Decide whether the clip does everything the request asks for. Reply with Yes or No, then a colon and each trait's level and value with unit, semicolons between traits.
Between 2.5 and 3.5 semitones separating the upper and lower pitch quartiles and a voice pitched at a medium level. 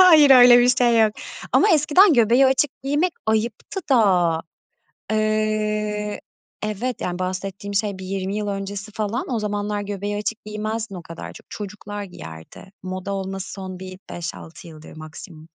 No: average, 3.1 semitones; high, 210 Hz